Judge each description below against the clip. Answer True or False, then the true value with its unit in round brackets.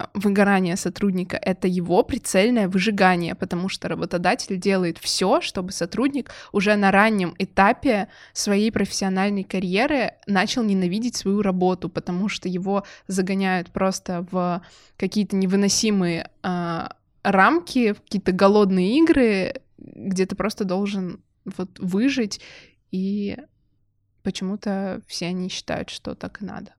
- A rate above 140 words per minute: False (115 wpm)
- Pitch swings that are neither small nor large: False (2.0 semitones)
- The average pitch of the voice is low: False (195 Hz)